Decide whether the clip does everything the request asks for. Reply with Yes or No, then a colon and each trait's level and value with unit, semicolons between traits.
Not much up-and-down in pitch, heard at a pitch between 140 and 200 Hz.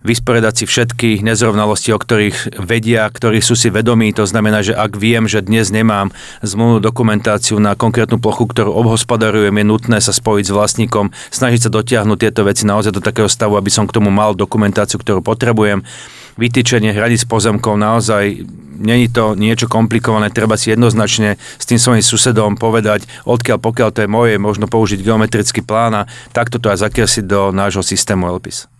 No: narrow, 1.7 semitones; low, 110 Hz